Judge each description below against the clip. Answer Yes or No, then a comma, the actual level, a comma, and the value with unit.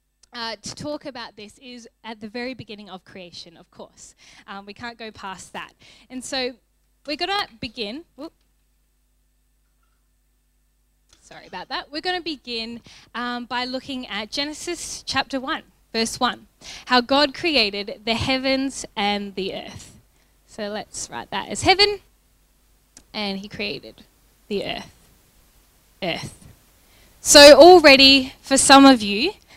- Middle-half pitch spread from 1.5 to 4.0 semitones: No, average, 4.6 semitones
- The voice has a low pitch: No, very high, 250 Hz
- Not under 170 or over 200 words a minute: No, average, 140 wpm